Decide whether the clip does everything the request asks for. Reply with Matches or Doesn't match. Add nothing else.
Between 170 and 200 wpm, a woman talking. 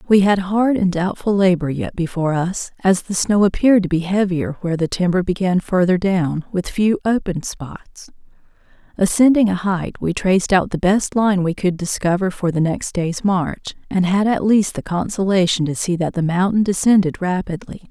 Matches